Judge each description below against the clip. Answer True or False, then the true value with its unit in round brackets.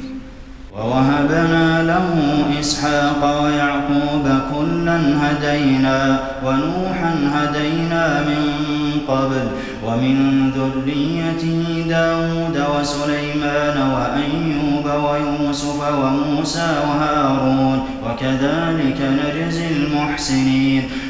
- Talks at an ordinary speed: False (60 wpm)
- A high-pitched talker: False (145 Hz)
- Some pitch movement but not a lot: False (1.9 semitones)